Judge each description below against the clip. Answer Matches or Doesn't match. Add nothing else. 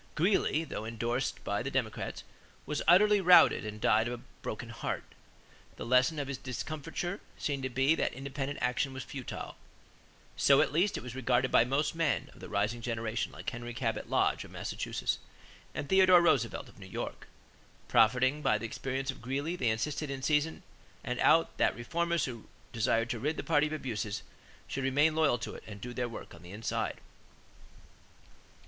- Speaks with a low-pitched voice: Matches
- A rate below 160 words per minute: Doesn't match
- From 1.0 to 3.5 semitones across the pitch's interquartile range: Doesn't match